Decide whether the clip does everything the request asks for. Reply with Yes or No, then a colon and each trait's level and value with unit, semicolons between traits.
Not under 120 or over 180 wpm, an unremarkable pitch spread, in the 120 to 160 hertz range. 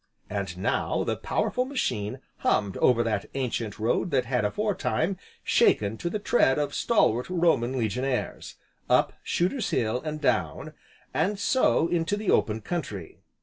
No: average, 145 wpm; wide, 8.0 semitones; low, 135 Hz